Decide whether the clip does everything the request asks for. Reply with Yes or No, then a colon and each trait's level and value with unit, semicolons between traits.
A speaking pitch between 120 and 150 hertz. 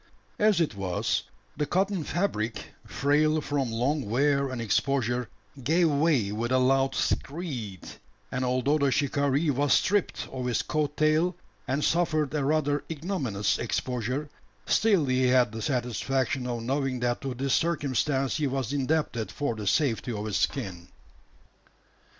Yes: low, 135 Hz